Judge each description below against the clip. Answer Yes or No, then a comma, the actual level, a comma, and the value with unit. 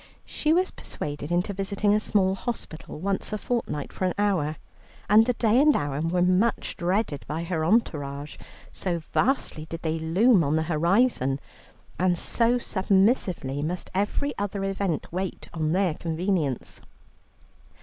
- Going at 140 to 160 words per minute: Yes, average, 150 wpm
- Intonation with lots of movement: No, average, 4.6 semitones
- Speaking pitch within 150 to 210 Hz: Yes, medium, 185 Hz